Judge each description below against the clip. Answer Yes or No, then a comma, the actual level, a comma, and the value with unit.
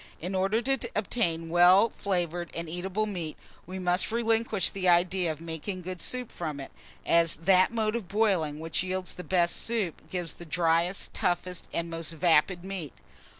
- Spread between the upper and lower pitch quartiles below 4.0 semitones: Yes, average, 2.8 semitones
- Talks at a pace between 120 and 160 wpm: No, average, 170 wpm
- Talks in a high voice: No, medium, 180 Hz